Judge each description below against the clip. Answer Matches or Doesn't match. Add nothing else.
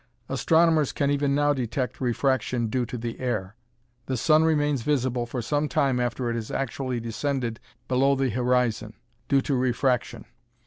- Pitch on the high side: Doesn't match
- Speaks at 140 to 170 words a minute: Matches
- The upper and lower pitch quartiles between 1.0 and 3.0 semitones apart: Matches